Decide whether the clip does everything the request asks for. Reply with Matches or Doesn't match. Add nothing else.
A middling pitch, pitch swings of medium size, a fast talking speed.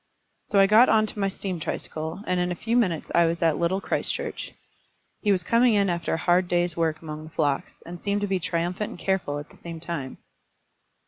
Matches